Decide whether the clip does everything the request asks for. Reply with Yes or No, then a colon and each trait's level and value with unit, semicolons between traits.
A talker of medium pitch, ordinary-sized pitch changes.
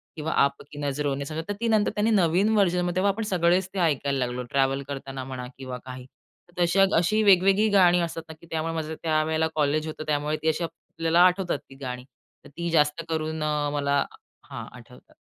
Yes: medium, 160 Hz; average, 3.9 semitones